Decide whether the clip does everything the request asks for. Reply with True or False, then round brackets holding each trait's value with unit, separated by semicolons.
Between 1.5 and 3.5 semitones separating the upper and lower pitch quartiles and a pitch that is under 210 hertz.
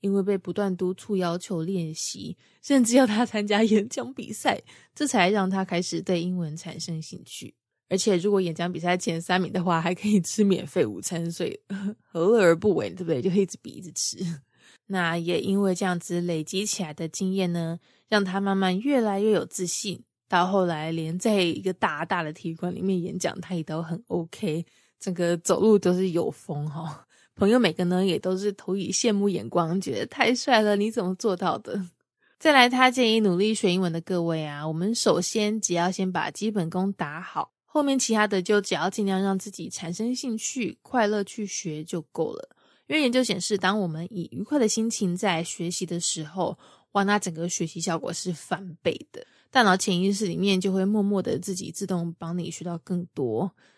True (3.2 semitones; 190 Hz)